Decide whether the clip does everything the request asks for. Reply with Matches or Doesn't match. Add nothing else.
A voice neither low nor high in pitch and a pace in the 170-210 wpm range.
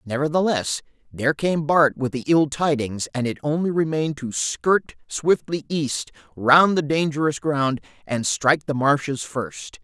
Doesn't match